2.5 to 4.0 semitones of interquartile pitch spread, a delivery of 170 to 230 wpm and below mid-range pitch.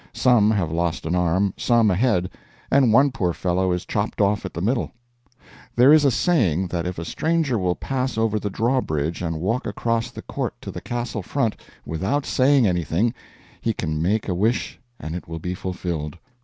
No: wide, 5.5 semitones; average, 195 wpm; low, 100 Hz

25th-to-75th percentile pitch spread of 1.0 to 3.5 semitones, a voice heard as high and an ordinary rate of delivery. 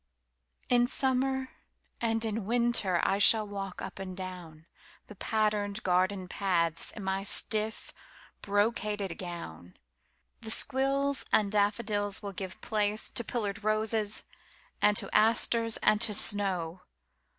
No: average, 2.9 semitones; high, 205 Hz; slow, 105 wpm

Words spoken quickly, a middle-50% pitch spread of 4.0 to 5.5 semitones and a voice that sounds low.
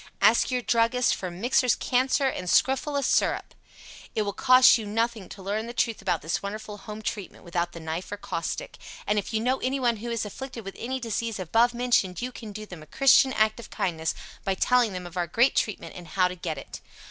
No: fast, 215 wpm; average, 4.7 semitones; high, 215 Hz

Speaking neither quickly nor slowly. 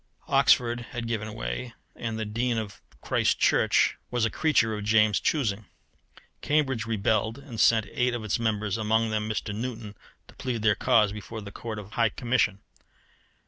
Yes: average, 170 wpm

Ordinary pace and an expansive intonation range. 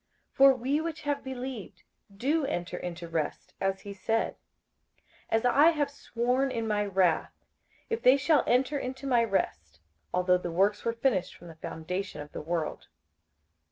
Yes: average, 165 wpm; wide, 6.8 semitones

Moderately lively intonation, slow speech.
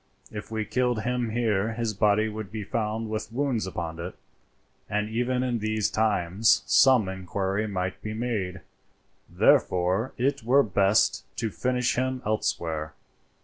No: average, 3.7 semitones; average, 145 wpm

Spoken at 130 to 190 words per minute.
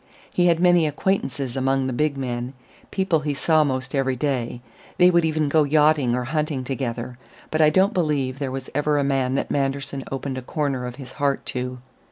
No: average, 200 wpm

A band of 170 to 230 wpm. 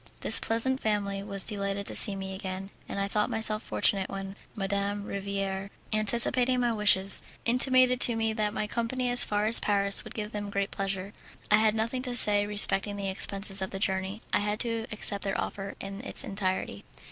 Yes: average, 195 wpm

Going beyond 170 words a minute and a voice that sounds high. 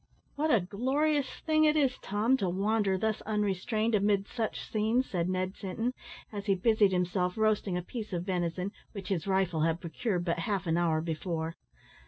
Yes: average, 180 wpm; high, 200 Hz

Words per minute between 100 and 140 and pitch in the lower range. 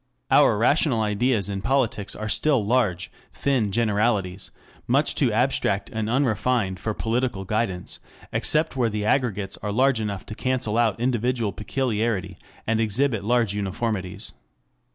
Yes: slow, 135 wpm; low, 110 Hz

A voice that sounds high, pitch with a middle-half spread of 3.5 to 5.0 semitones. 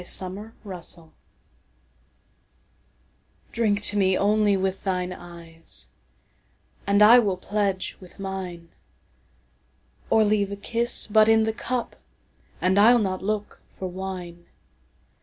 No: high, 195 Hz; average, 2.8 semitones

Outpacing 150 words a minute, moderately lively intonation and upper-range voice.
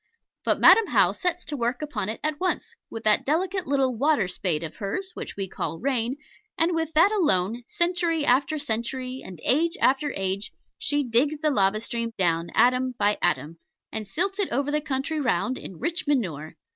No: average, 185 wpm; wide, 6.8 semitones; very high, 260 Hz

